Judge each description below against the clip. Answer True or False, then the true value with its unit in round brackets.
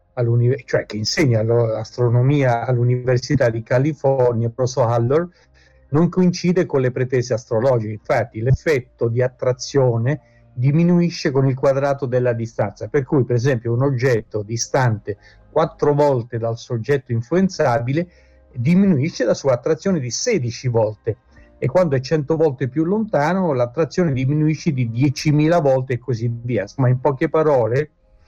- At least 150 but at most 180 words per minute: False (135 wpm)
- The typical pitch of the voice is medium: False (130 Hz)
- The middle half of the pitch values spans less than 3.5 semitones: False (4.3 semitones)